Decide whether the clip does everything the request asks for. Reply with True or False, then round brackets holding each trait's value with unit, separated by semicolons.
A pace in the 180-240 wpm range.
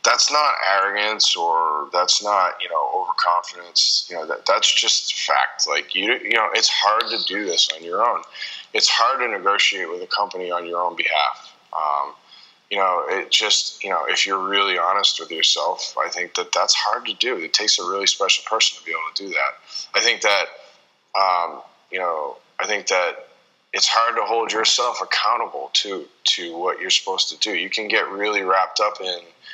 True (200 wpm)